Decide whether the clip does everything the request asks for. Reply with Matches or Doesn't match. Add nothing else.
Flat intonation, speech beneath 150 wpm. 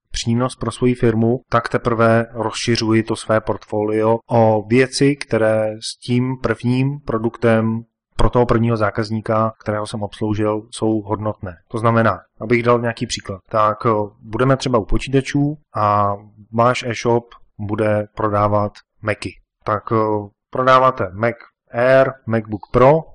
Matches